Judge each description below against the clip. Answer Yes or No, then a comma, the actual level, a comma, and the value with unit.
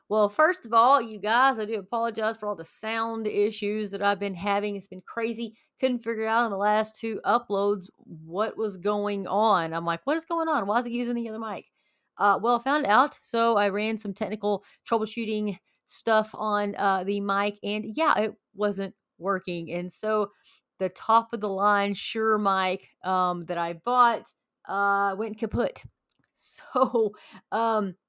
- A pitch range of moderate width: No, narrow, 2.3 semitones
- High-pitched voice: Yes, high, 210 Hz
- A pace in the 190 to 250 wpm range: No, average, 180 wpm